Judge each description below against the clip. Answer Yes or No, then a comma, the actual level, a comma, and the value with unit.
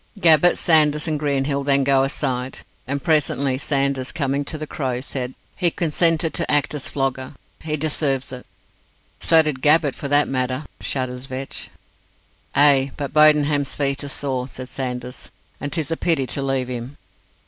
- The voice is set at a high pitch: No, medium, 140 Hz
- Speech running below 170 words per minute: Yes, average, 160 wpm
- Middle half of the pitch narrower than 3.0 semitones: Yes, narrow, 2.4 semitones